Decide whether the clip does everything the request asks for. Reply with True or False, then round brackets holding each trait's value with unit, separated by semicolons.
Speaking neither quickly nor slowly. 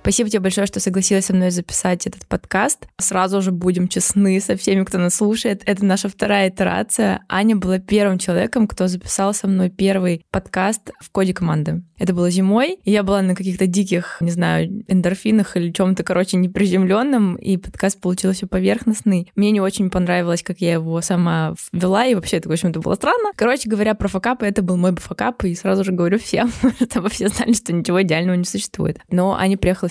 False (195 wpm)